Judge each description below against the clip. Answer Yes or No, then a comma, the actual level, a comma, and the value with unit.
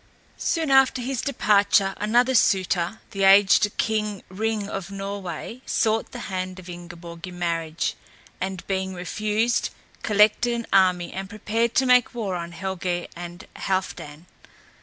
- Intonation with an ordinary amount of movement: Yes, average, 3.7 semitones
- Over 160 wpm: No, average, 140 wpm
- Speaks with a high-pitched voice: Yes, high, 195 Hz